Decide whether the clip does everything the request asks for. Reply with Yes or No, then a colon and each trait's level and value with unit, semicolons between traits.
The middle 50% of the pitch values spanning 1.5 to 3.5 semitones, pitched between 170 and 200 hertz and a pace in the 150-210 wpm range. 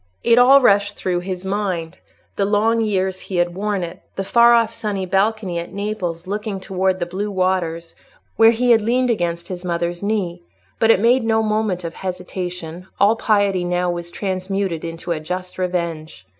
Yes: average, 3.2 semitones; high, 190 Hz; average, 175 wpm